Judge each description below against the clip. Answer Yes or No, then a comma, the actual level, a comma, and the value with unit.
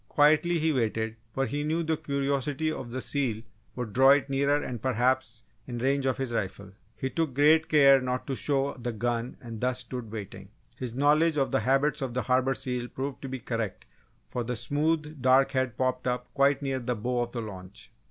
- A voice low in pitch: Yes, low, 130 Hz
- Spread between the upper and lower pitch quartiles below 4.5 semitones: Yes, average, 2.8 semitones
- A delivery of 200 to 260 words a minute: Yes, fast, 205 wpm